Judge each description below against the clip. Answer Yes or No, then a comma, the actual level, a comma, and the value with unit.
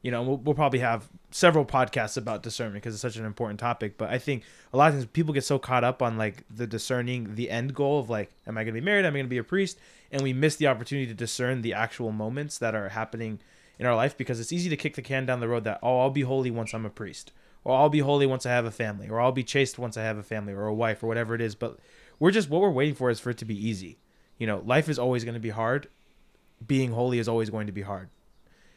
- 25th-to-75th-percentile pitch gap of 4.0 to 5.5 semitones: No, average, 3.4 semitones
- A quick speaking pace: Yes, fast, 290 wpm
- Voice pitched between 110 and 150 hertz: Yes, low, 120 Hz